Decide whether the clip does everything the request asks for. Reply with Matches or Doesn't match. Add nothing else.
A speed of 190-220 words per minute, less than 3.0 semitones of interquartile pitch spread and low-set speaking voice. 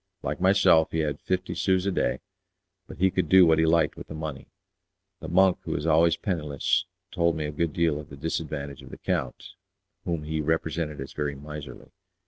Matches